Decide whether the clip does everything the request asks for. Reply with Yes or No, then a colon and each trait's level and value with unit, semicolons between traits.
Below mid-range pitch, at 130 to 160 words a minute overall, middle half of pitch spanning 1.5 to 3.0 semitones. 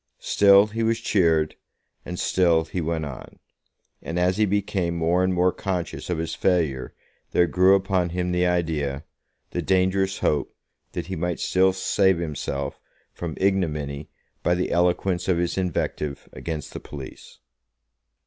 Yes: very low, 90 Hz; average, 150 wpm; narrow, 2.6 semitones